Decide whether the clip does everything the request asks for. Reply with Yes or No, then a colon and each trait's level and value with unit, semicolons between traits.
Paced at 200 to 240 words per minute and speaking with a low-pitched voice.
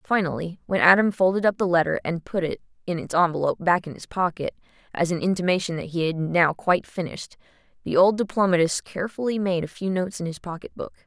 No: fast, 205 wpm; medium, 180 Hz